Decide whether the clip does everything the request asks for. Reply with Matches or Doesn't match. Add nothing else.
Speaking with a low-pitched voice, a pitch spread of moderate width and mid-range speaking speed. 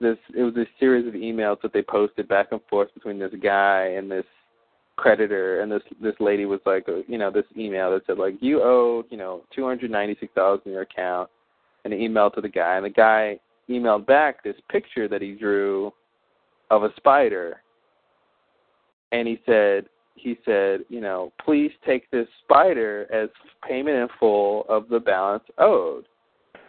Matches